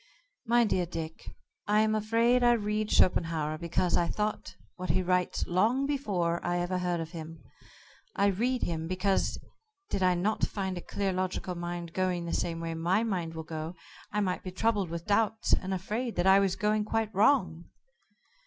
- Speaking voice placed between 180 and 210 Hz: Yes, medium, 185 Hz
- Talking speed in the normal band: Yes, average, 180 wpm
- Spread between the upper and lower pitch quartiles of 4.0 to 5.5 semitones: No, average, 3.6 semitones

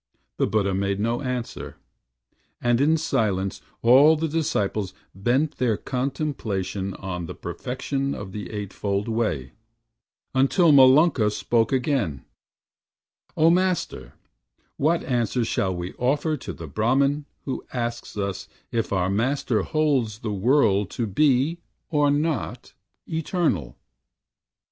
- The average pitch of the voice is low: Yes, low, 120 Hz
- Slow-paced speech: Yes, slow, 120 wpm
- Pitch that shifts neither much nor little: No, wide, 6.3 semitones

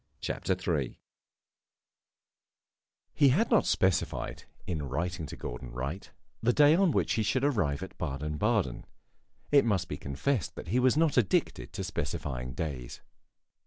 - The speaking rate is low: No, average, 145 wpm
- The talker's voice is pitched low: Yes, very low, 90 Hz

